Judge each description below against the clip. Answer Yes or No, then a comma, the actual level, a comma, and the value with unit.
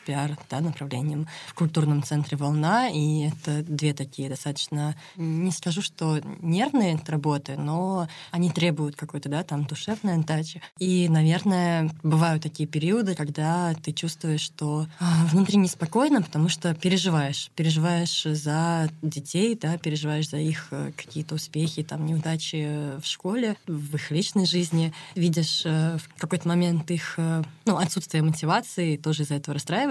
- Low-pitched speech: No, medium, 160 Hz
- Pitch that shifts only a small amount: Yes, narrow, 2.3 semitones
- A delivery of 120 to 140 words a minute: Yes, average, 135 wpm